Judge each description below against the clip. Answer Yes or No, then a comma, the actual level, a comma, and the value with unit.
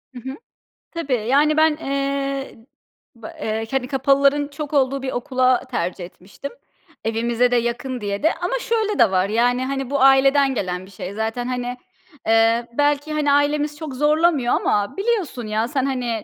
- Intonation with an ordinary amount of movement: Yes, average, 3.7 semitones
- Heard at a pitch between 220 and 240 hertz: No, very high, 265 Hz